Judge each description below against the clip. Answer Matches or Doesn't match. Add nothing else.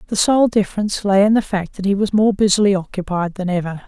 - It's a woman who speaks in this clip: Matches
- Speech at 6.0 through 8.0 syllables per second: Matches